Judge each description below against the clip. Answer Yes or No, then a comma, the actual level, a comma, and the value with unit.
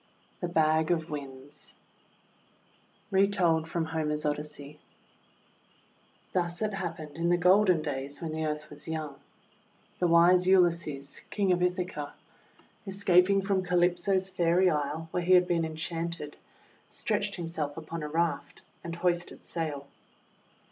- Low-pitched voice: No, medium, 170 Hz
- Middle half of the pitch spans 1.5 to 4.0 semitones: Yes, average, 2.9 semitones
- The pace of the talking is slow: Yes, slow, 130 wpm